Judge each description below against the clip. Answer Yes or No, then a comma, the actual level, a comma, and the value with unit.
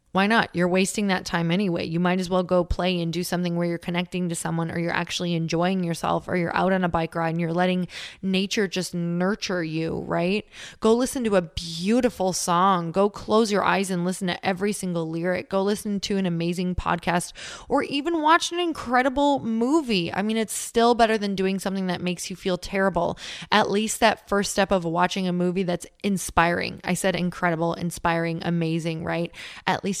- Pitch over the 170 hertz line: Yes, medium, 185 Hz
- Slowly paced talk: No, average, 200 wpm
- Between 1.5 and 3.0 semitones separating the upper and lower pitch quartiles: Yes, narrow, 2.5 semitones